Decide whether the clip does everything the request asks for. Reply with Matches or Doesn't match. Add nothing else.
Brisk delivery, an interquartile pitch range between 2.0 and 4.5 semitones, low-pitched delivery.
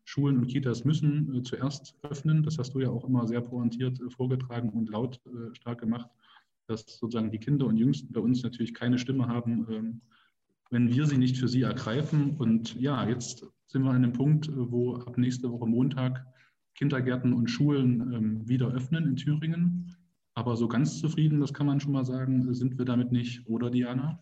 Matches